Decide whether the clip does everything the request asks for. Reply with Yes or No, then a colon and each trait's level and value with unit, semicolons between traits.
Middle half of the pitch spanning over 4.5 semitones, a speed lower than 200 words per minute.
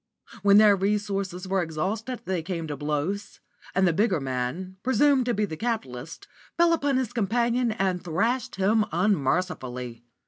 Yes: wide, 5.5 semitones; average, 150 wpm